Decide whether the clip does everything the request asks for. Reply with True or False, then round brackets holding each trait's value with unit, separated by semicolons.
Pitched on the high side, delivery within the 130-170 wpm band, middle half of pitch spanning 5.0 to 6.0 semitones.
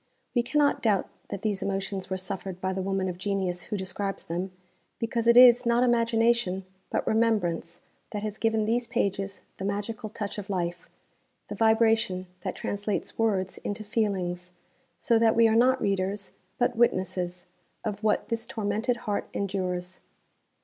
False (205 Hz; 160 wpm; 3.3 semitones)